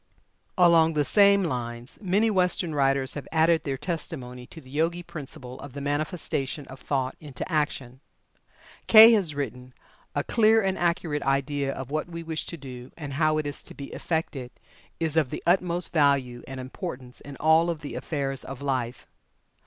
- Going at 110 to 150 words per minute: No, average, 170 wpm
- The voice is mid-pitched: Yes, medium, 145 Hz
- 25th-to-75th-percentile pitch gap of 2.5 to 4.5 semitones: Yes, average, 4.0 semitones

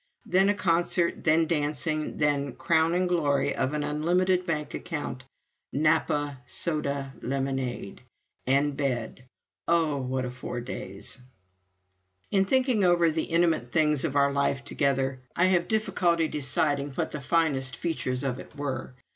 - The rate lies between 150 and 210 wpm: No, average, 140 wpm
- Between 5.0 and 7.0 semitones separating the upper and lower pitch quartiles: No, average, 3.8 semitones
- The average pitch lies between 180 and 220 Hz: No, medium, 150 Hz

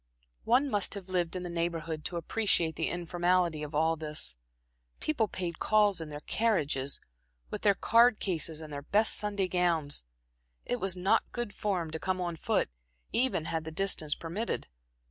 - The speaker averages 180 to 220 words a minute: No, average, 170 wpm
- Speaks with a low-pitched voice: No, medium, 175 Hz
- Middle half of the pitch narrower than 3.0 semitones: No, average, 4.1 semitones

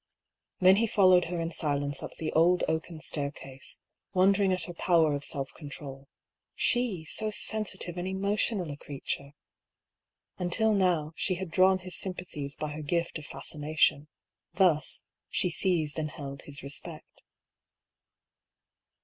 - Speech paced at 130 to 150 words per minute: Yes, average, 140 wpm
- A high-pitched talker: No, medium, 170 Hz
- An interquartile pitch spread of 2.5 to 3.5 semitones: No, average, 4.0 semitones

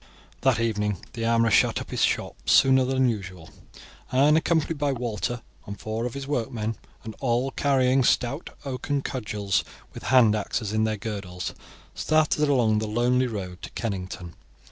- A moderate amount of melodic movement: Yes, average, 3.8 semitones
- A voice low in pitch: Yes, low, 115 Hz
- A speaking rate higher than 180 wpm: No, average, 160 wpm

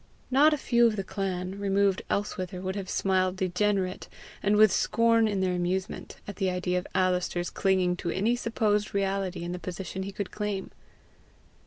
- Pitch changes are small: Yes, narrow, 2.2 semitones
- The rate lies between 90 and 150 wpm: No, average, 175 wpm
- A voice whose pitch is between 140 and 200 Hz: Yes, high, 190 Hz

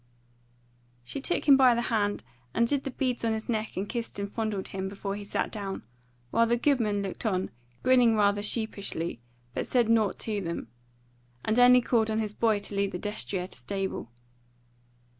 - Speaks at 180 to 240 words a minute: Yes, average, 185 wpm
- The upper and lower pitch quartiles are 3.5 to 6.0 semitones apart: No, average, 2.8 semitones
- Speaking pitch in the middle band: No, high, 215 Hz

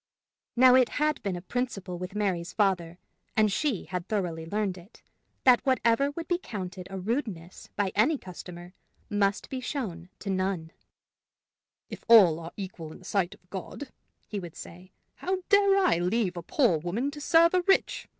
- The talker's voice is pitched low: No, high, 195 Hz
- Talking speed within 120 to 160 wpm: No, average, 175 wpm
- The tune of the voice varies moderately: No, wide, 6.1 semitones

